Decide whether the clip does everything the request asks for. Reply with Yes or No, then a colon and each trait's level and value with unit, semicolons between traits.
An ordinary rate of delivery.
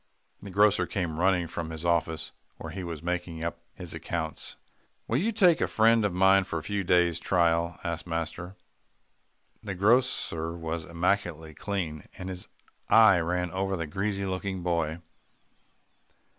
Yes: average, 155 wpm